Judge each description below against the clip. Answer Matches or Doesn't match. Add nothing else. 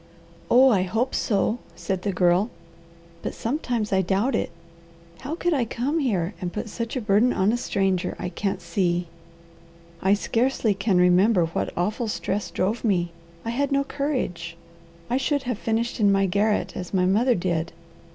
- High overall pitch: Matches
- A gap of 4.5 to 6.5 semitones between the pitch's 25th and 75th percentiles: Matches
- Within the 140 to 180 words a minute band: Matches